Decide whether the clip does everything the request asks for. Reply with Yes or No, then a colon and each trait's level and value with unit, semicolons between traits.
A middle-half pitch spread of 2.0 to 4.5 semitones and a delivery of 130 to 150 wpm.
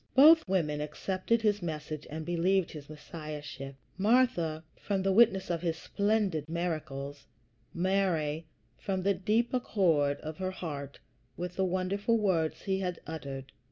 Yes: average, 4.2 semitones; average, 140 wpm